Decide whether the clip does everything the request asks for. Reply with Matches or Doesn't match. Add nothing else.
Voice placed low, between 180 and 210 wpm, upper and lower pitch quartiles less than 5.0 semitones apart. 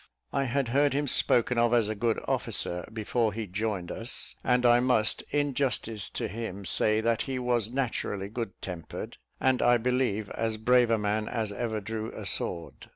Matches